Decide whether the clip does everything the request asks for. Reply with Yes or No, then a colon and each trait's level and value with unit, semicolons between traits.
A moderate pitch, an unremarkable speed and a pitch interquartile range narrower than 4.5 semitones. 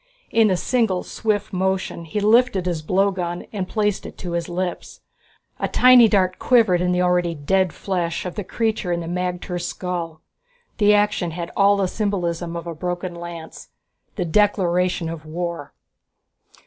Yes: medium, 180 Hz; average, 160 wpm; average, 2.8 semitones